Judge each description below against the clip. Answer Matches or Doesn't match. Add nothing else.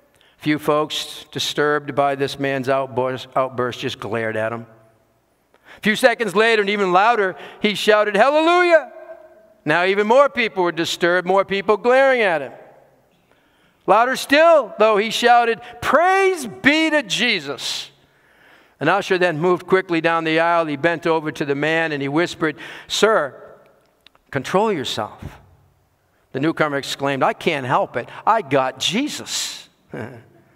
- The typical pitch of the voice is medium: Matches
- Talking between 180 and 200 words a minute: Doesn't match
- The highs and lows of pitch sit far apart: Matches